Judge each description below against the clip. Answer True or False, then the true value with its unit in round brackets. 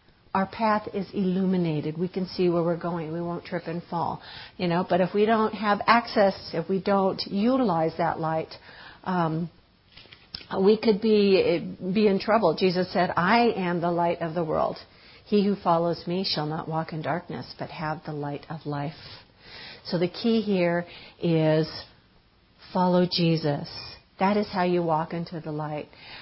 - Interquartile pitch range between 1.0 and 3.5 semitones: True (3.1 semitones)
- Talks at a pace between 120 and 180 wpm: True (170 wpm)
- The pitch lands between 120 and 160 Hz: False (175 Hz)